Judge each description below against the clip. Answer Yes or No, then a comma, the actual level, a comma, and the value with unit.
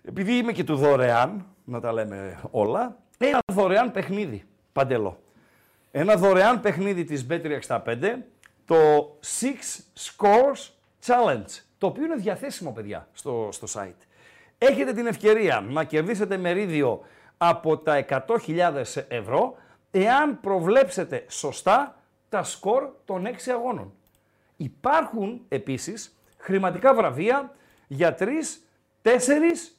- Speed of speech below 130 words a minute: Yes, slow, 115 wpm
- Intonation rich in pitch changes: Yes, wide, 7.9 semitones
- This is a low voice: No, high, 200 Hz